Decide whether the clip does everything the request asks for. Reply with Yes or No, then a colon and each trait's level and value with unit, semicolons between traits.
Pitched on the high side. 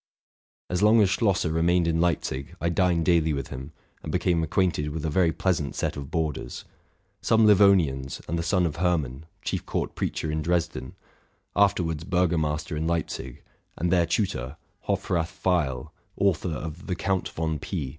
No: very low, 85 Hz